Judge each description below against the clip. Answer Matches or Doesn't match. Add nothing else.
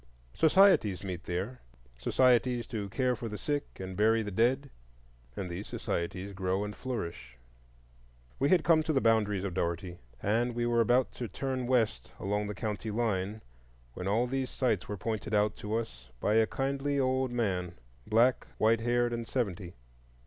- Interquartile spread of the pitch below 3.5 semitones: Doesn't match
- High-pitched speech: Doesn't match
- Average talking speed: Matches